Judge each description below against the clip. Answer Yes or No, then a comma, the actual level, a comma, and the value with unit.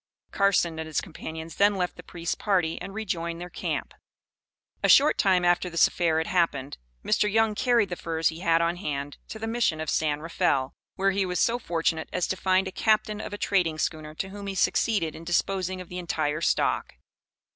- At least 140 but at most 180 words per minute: No, fast, 205 wpm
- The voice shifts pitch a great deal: No, average, 3.4 semitones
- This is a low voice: No, medium, 175 Hz